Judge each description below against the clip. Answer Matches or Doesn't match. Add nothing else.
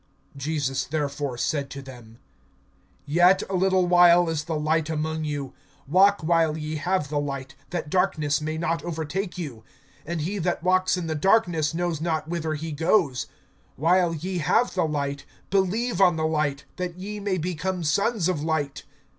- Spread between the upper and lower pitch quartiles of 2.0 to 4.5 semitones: Matches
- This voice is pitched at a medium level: Matches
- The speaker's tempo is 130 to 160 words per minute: Doesn't match